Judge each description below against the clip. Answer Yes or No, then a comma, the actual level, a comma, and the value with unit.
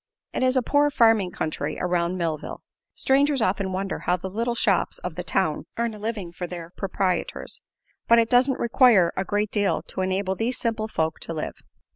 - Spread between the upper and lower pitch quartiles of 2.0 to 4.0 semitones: No, average, 4.5 semitones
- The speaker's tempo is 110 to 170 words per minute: No, average, 190 wpm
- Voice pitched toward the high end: Yes, high, 195 Hz